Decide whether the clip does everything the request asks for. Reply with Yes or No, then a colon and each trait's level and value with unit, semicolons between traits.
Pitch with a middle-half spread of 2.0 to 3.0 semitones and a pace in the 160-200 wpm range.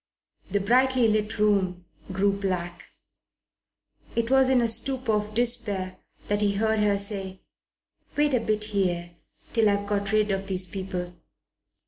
No: narrow, 2.6 semitones; average, 145 wpm